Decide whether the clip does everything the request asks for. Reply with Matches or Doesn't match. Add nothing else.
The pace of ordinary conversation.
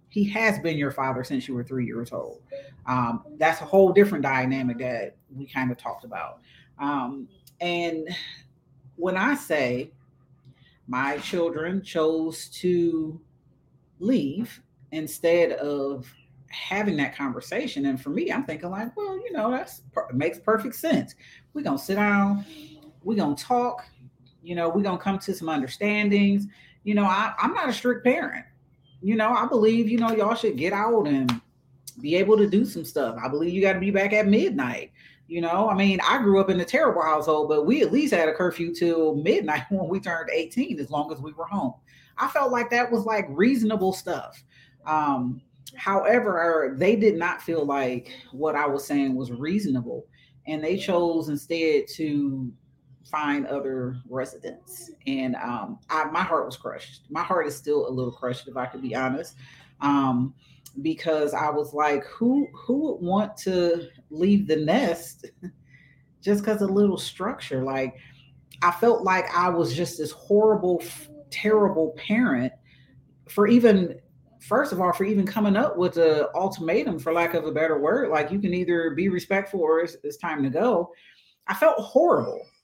Matches